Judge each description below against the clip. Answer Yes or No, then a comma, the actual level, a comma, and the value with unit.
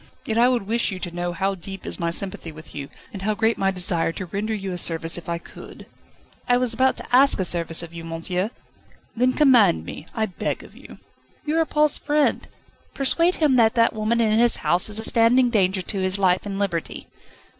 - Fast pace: Yes, fast, 220 wpm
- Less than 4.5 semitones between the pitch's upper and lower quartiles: No, average, 5.1 semitones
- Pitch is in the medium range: No, high, 200 Hz